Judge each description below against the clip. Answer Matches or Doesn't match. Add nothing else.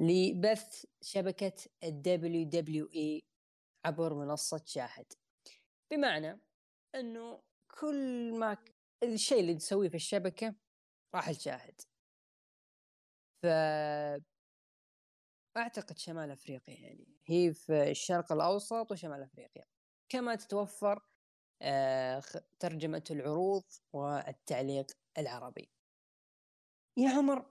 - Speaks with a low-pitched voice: Doesn't match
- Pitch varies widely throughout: Matches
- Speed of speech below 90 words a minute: Matches